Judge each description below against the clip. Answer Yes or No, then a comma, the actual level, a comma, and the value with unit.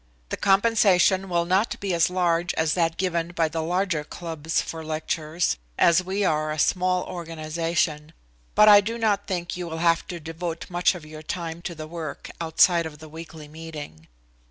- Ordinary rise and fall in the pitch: No, narrow, 2.2 semitones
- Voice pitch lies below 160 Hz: No, medium, 170 Hz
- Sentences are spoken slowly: No, average, 180 wpm